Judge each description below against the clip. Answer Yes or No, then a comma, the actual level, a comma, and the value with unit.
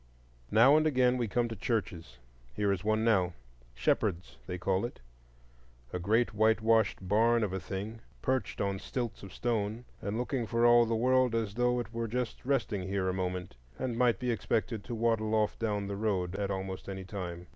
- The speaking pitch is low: Yes, low, 105 Hz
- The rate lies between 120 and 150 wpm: No, average, 185 wpm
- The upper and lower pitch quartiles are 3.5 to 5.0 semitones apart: Yes, average, 3.9 semitones